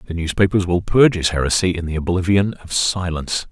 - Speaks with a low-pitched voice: Yes, very low, 90 Hz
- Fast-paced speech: No, average, 190 wpm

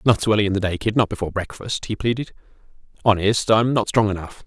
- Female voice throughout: No, male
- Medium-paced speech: No, fast, 230 wpm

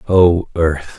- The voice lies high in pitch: No, very low, 85 Hz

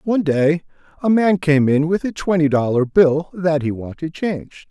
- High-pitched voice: No, medium, 160 Hz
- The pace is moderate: Yes, average, 190 wpm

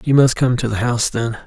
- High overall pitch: No, low, 120 Hz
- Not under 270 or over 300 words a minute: Yes, fast, 285 wpm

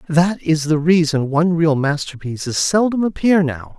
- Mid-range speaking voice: Yes, medium, 160 Hz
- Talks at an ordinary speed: Yes, average, 160 wpm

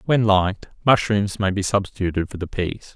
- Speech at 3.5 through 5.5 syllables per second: Yes, 5.3 syllables/s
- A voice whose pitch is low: Yes, low, 100 Hz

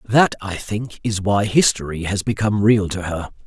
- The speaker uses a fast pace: No, average, 190 wpm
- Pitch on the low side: Yes, low, 100 Hz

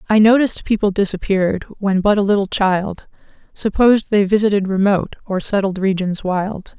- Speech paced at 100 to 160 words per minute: Yes, average, 150 wpm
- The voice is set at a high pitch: Yes, high, 200 Hz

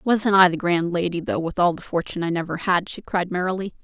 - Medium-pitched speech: Yes, medium, 180 Hz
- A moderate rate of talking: No, fast, 250 wpm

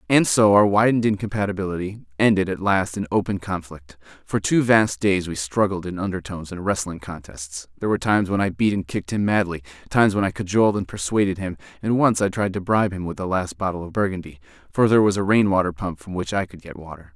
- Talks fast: Yes, fast, 225 wpm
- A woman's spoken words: No, male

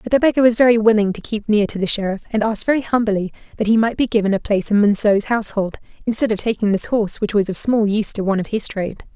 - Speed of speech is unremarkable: No, fast, 270 wpm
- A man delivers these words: No, female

